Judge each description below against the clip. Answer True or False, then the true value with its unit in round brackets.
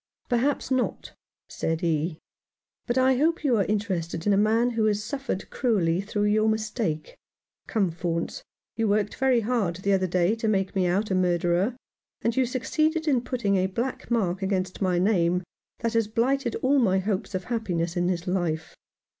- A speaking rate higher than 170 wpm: True (185 wpm)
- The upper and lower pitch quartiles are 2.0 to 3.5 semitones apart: False (4.6 semitones)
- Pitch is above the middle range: True (205 Hz)